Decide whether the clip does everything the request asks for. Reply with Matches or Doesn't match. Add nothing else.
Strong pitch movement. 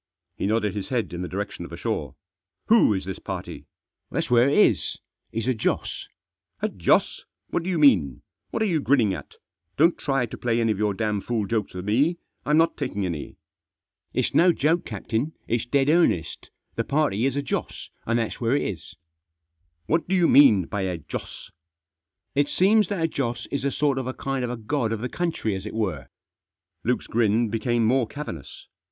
Matches